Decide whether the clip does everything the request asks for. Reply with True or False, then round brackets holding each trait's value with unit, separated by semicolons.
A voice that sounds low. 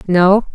False (190 Hz)